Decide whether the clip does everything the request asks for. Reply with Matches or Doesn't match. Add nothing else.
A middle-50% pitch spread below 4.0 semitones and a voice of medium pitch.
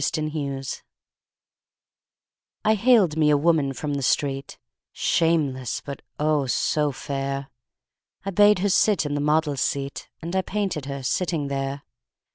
Matches